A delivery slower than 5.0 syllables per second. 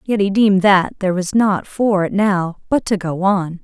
Yes: 4.7 syllables/s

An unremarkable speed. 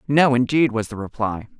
Yes: average, 190 wpm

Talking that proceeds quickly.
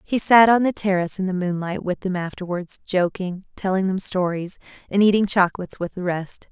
No: average, 195 wpm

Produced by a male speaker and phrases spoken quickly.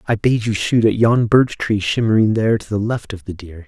Yes: male; fast, 260 wpm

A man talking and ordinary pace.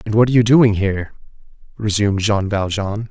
Yes: male; average, 175 wpm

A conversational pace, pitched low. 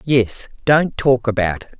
Yes: average, 165 wpm; low, 120 Hz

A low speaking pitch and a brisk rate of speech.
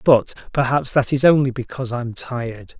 No: low, 125 Hz; average, 170 wpm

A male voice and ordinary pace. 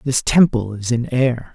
Yes: male; average, 195 wpm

